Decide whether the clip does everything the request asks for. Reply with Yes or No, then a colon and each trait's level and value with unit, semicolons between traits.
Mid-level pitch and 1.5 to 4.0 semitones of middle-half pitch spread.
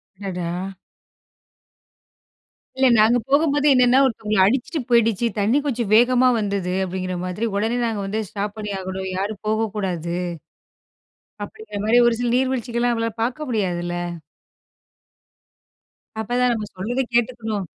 No: high, 220 Hz; average, 3.5 semitones